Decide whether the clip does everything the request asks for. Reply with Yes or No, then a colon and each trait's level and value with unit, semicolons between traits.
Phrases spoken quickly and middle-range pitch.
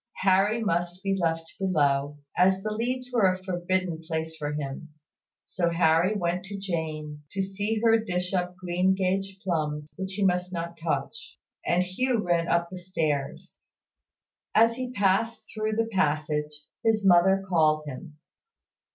No: average, 150 wpm; medium, 180 Hz